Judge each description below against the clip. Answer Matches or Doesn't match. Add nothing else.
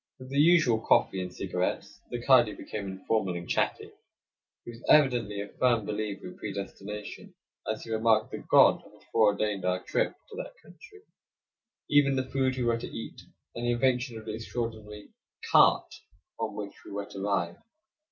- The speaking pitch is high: Doesn't match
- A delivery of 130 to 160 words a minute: Doesn't match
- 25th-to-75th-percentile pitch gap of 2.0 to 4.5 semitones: Matches